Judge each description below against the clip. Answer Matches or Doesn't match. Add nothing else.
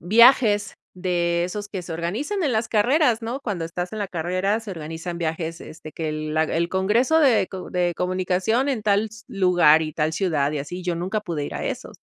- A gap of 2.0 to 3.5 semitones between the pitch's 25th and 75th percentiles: Doesn't match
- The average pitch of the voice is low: Doesn't match